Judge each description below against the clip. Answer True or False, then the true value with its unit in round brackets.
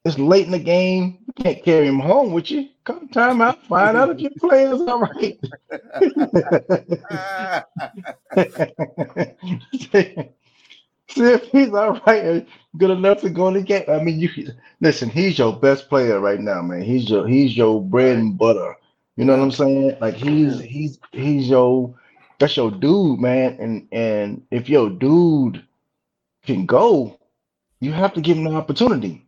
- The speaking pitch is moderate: True (165 Hz)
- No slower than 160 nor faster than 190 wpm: True (170 wpm)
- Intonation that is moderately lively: False (7.2 semitones)